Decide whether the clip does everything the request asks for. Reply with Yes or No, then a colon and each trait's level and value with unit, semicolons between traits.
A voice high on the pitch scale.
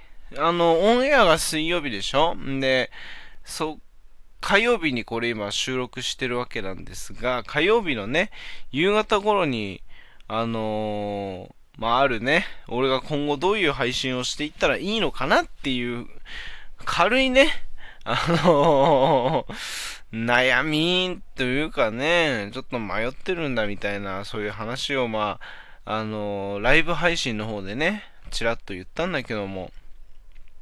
No: low, 125 Hz